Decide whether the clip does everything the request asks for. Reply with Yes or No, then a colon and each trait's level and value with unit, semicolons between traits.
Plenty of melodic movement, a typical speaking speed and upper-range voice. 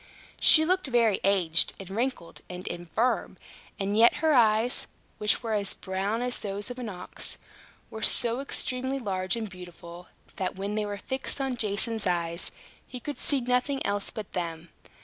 No: average, 4.9 semitones; average, 170 wpm; high, 210 Hz